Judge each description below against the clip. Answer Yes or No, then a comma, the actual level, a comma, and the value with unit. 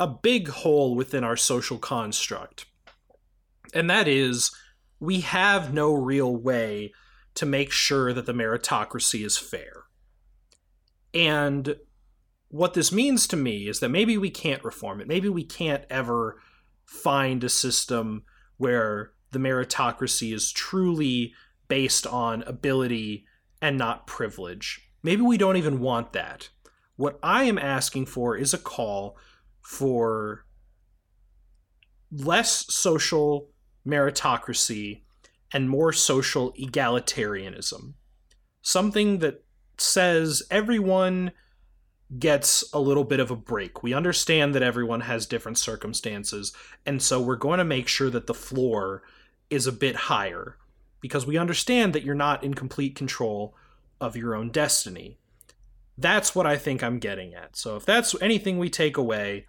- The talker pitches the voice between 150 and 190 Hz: No, low, 135 Hz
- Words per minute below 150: Yes, slow, 135 wpm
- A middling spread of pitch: Yes, average, 4.8 semitones